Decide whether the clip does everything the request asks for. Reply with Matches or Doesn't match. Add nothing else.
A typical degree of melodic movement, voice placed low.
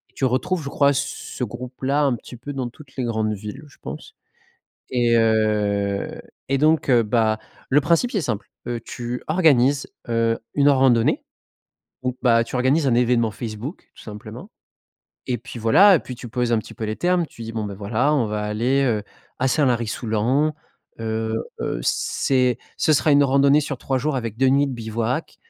Matches